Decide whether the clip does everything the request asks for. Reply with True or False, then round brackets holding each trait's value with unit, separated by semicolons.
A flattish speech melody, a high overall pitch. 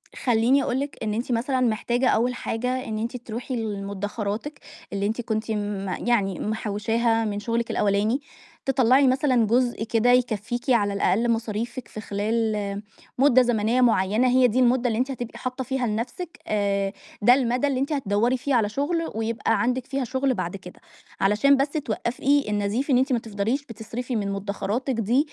False (3.3 semitones; 235 Hz)